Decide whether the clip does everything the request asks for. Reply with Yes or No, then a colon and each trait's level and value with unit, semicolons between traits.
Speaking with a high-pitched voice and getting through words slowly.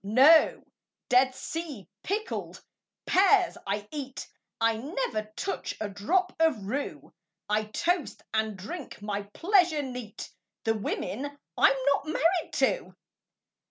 Yes: very high, 270 Hz; slow, 120 wpm